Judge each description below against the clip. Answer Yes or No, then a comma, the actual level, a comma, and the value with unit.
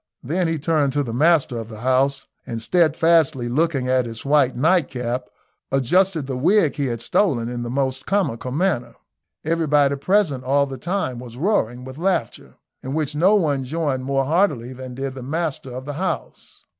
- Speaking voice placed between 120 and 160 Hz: Yes, medium, 140 Hz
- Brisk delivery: No, average, 180 wpm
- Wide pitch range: No, average, 4.4 semitones